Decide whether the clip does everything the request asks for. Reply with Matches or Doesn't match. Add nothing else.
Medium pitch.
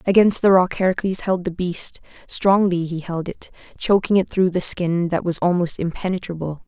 Matches